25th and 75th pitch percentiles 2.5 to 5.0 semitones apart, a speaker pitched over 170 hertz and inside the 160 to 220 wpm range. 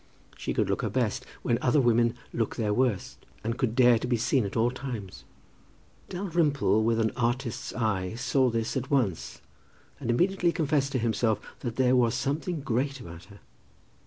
No: average, 3.1 semitones; low, 120 Hz; average, 175 wpm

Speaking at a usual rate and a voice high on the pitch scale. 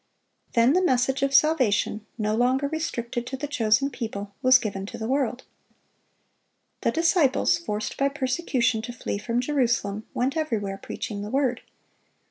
Yes: average, 150 wpm; very high, 250 Hz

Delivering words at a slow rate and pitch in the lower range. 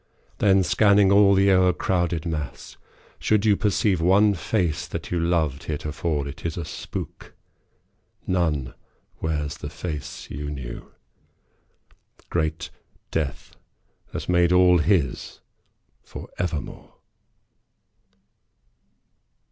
Yes: slow, 100 wpm; very low, 85 Hz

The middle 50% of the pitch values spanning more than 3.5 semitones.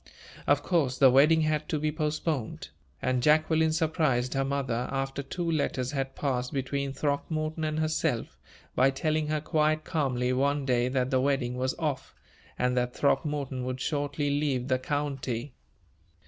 No: average, 3.1 semitones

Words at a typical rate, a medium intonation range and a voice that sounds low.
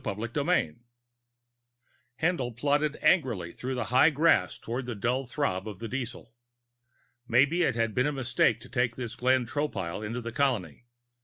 Yes: average, 155 wpm; average, 3.7 semitones; low, 125 Hz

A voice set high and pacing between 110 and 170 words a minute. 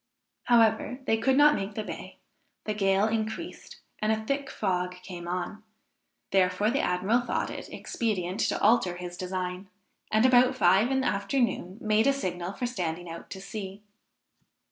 Yes: high, 205 Hz; average, 160 wpm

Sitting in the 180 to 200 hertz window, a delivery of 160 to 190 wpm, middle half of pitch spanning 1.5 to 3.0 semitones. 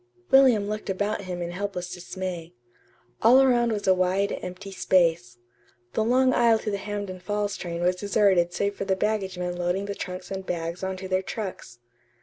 Yes: high, 190 Hz; average, 185 wpm; narrow, 2.5 semitones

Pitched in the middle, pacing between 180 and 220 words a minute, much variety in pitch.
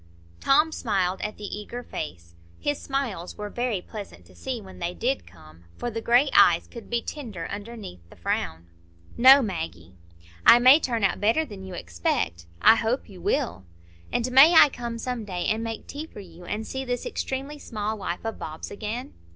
No: high, 220 Hz; average, 190 wpm; wide, 5.8 semitones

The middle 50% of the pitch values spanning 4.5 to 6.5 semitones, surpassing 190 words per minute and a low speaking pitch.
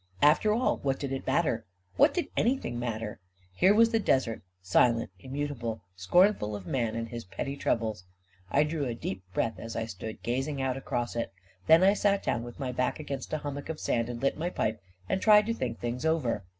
Yes: average, 5.2 semitones; fast, 205 wpm; low, 130 Hz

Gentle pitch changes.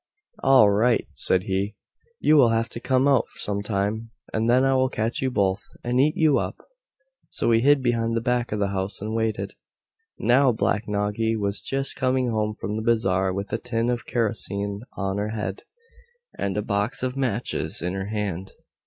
No: average, 3.3 semitones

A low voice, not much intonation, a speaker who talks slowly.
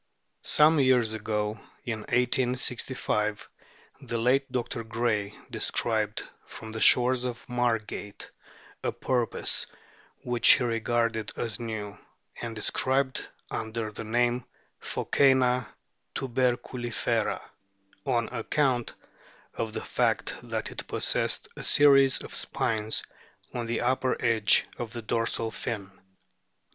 Yes: low, 120 Hz; narrow, 2.3 semitones; slow, 115 wpm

